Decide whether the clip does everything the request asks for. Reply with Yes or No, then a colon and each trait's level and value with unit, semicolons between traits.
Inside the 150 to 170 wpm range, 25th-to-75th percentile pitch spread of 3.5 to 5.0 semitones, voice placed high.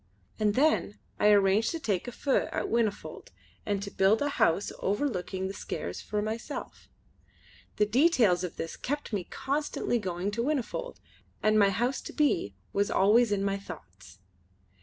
Yes: average, 160 wpm; average, 4.0 semitones; high, 210 Hz